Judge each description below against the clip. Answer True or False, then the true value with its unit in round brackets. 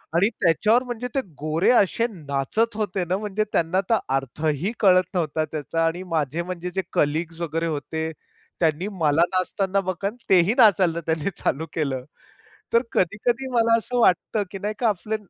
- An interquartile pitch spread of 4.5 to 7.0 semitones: True (4.8 semitones)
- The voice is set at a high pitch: False (180 Hz)